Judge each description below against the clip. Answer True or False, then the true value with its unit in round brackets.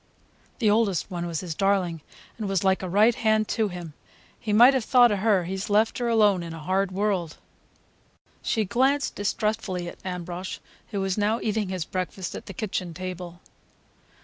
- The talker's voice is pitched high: True (195 Hz)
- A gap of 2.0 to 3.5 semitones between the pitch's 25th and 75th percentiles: True (3.2 semitones)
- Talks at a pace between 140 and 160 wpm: False (180 wpm)